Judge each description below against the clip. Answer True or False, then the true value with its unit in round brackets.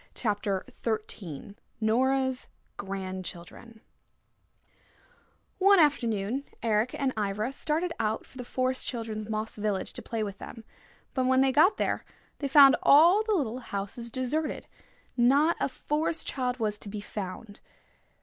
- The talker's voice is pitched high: True (235 Hz)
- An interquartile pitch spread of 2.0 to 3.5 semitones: False (4.4 semitones)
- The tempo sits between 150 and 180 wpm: False (135 wpm)